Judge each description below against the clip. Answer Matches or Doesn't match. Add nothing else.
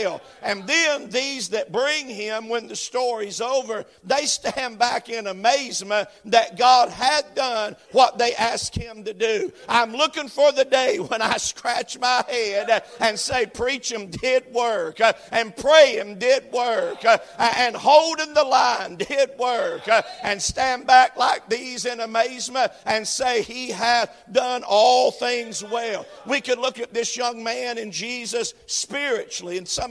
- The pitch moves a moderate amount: Matches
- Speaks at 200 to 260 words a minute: Doesn't match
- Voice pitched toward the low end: Doesn't match